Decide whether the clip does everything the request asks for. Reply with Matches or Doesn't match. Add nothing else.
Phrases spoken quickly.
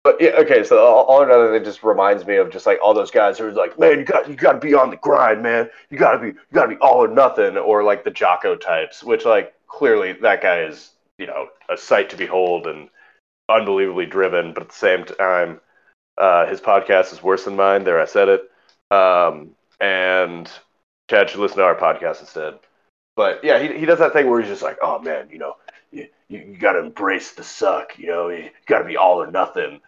Matches